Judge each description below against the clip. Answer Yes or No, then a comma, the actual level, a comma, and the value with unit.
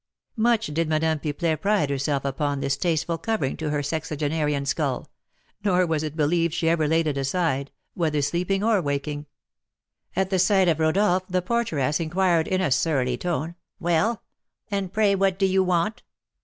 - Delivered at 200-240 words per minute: No, average, 170 wpm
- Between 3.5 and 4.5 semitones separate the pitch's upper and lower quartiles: Yes, average, 4.0 semitones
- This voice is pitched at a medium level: Yes, medium, 165 Hz